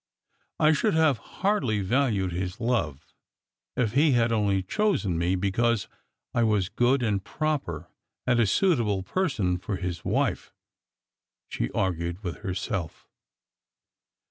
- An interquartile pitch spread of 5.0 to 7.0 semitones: Yes, wide, 5.6 semitones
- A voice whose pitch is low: Yes, low, 105 Hz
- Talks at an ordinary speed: No, slow, 125 wpm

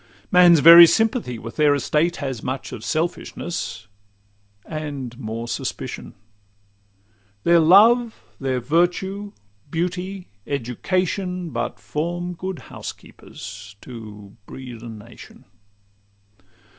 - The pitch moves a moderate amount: No, wide, 6.7 semitones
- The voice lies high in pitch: No, medium, 155 Hz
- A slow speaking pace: Yes, slow, 95 wpm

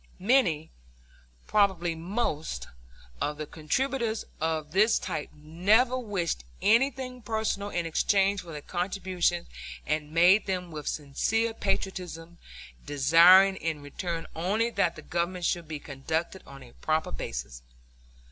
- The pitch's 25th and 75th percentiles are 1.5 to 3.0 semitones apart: No, average, 4.5 semitones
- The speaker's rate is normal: No, slow, 125 wpm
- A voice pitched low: No, medium, 175 Hz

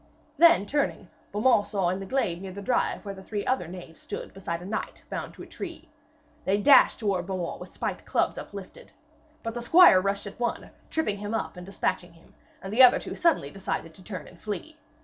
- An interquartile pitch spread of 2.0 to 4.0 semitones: No, average, 4.7 semitones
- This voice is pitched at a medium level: No, high, 200 Hz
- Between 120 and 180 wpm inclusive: No, fast, 205 wpm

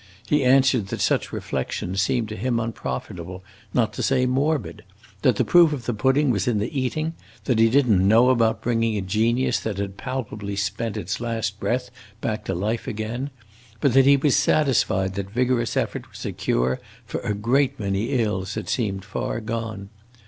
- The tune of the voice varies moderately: Yes, average, 4.2 semitones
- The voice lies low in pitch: Yes, low, 115 Hz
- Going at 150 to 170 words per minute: No, average, 185 wpm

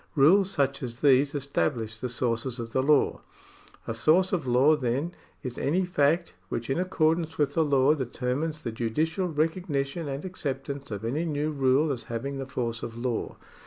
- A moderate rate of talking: Yes, average, 175 wpm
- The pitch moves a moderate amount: Yes, average, 3.9 semitones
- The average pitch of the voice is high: No, medium, 140 Hz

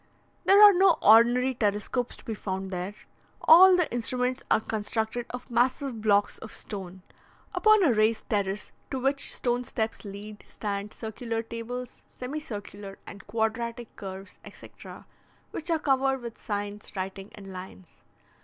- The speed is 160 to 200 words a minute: No, average, 145 wpm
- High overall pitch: Yes, high, 225 Hz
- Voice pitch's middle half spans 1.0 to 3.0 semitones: No, average, 3.7 semitones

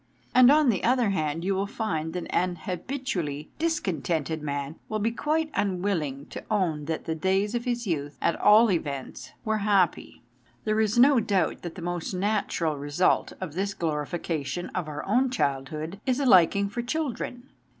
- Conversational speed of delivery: Yes, average, 175 wpm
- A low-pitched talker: No, medium, 185 Hz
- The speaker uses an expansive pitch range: Yes, wide, 5.8 semitones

